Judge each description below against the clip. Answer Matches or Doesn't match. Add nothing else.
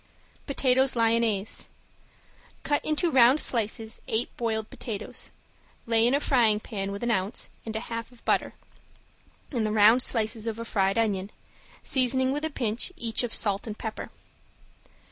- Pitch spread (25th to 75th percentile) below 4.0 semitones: Matches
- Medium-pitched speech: Doesn't match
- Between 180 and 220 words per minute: Doesn't match